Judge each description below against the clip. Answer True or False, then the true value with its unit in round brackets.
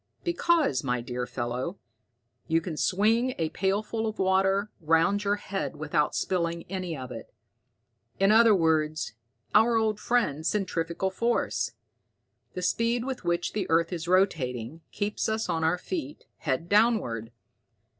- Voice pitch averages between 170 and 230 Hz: True (185 Hz)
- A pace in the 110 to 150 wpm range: True (140 wpm)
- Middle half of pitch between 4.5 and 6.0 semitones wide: True (5.2 semitones)